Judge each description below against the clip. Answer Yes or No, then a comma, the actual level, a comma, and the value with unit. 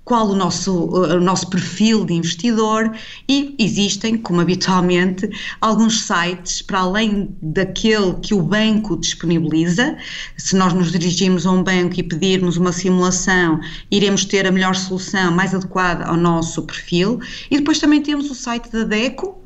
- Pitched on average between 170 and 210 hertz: Yes, high, 190 Hz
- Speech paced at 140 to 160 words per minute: Yes, average, 155 wpm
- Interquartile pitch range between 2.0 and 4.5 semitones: Yes, average, 3.6 semitones